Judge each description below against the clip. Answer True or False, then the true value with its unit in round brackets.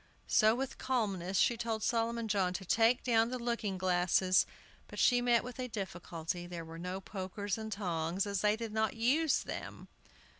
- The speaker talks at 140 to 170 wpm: False (180 wpm)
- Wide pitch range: False (4.1 semitones)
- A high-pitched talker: True (210 Hz)